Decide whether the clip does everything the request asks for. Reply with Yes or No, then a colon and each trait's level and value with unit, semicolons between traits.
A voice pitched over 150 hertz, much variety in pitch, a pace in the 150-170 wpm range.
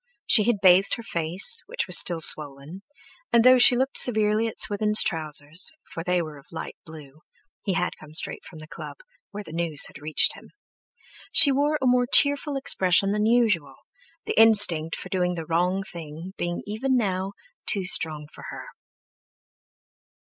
Yes: medium, 185 Hz; wide, 5.7 semitones; average, 165 wpm